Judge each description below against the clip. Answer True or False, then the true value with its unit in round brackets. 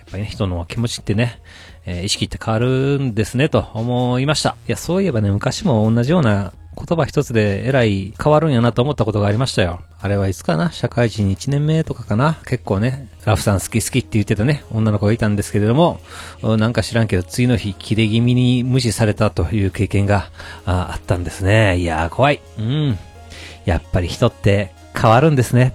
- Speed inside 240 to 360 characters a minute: False (400 characters per minute)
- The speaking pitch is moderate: False (110 Hz)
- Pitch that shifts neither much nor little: True (4.1 semitones)